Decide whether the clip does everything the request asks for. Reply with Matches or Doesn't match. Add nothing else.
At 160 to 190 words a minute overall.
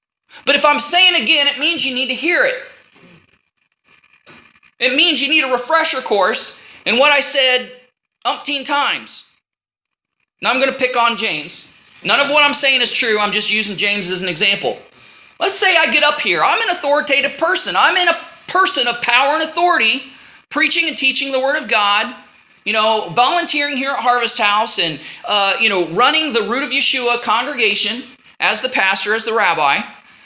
Matches